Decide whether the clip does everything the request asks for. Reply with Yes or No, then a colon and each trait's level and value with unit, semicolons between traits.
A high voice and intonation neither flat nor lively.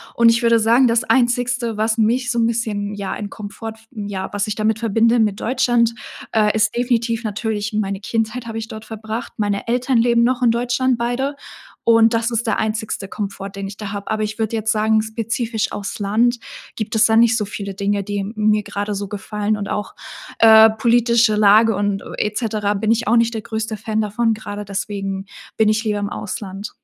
No: high, 220 Hz; narrow, 2.0 semitones